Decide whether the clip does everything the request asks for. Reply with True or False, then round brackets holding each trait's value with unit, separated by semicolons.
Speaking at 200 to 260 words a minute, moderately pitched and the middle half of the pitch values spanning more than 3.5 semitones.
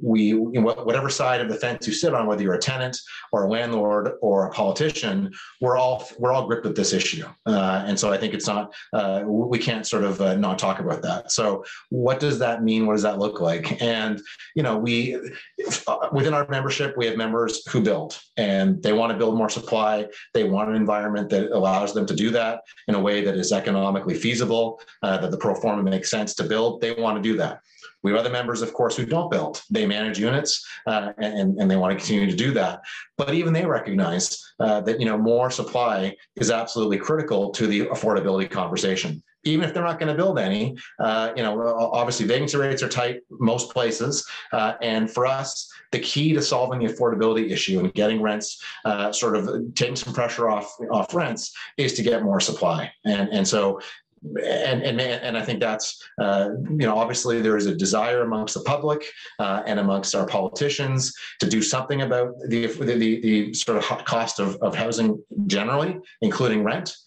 False (205 wpm; 115 Hz; 4.0 semitones)